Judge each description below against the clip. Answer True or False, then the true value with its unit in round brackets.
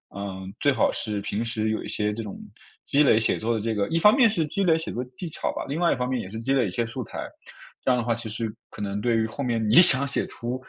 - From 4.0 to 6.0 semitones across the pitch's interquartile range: True (4.3 semitones)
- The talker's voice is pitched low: True (115 Hz)